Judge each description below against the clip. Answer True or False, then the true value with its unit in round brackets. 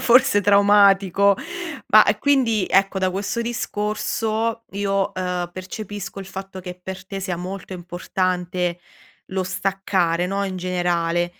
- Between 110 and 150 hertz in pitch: False (195 Hz)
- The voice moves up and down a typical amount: False (2.1 semitones)